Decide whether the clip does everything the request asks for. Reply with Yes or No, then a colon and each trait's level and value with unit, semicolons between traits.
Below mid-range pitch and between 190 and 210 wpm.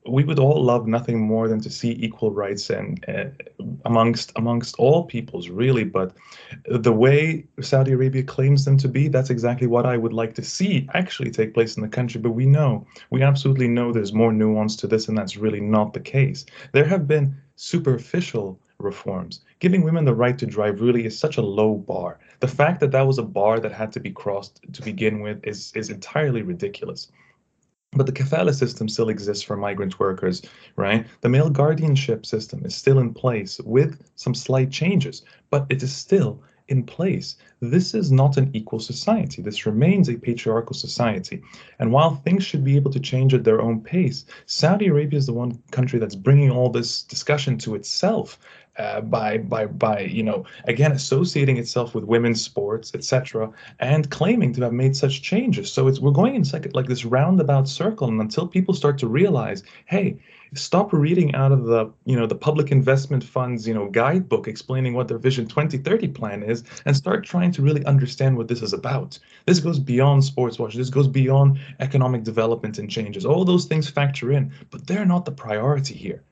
Yes: low, 130 Hz; average, 195 wpm